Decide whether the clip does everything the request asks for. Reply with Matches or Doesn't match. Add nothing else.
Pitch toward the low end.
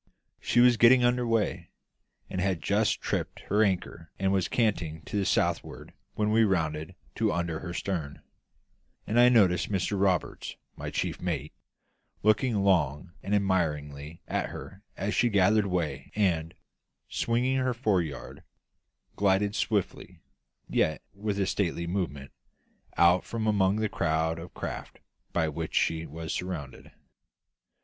Matches